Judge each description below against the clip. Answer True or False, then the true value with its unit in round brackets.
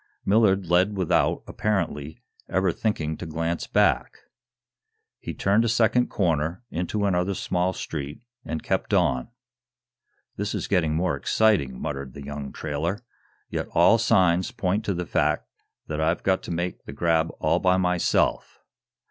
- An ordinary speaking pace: True (150 wpm)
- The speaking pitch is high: False (90 Hz)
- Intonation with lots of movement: False (3.7 semitones)